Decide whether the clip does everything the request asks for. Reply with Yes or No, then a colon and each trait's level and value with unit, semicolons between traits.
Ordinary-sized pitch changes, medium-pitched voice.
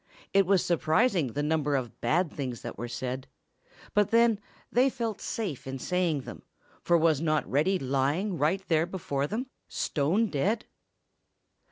No: wide, 5.8 semitones; medium, 160 Hz